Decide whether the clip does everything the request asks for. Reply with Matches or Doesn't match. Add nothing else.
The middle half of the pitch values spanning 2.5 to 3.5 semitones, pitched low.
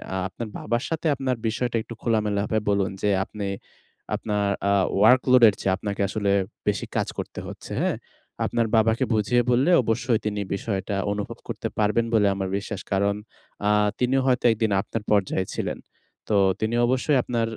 Matches